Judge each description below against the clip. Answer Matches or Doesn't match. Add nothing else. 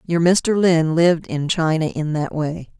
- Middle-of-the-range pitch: Matches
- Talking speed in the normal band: Matches